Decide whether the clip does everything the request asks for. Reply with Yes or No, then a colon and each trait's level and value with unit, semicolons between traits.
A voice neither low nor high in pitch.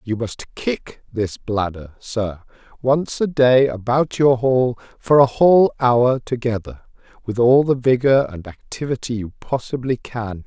No: low, 120 Hz